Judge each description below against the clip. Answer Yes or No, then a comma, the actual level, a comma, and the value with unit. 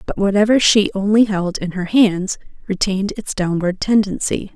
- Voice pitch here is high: Yes, high, 200 Hz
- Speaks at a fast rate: No, average, 160 wpm